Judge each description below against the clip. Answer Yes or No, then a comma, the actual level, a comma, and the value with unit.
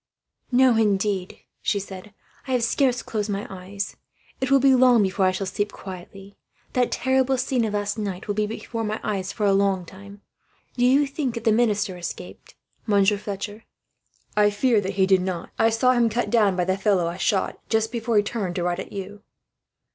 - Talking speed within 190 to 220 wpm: Yes, average, 200 wpm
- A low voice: No, high, 205 Hz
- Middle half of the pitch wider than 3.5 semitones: No, average, 3.2 semitones